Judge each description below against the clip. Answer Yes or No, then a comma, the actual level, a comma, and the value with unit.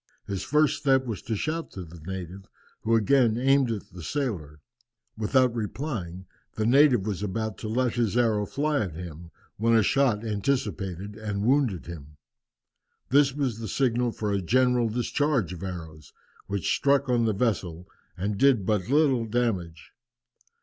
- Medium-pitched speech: No, low, 110 Hz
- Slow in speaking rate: No, average, 160 wpm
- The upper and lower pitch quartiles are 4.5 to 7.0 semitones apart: Yes, average, 5.2 semitones